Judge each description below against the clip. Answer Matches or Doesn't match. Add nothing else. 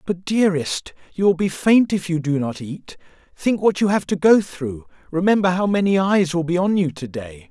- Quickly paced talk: Matches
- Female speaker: Doesn't match